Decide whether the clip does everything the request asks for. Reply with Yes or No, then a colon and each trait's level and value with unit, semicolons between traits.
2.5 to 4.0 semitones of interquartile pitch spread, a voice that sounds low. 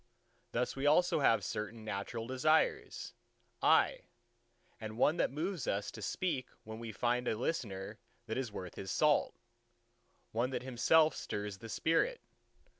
No: average, 5.2 semitones; low, 120 Hz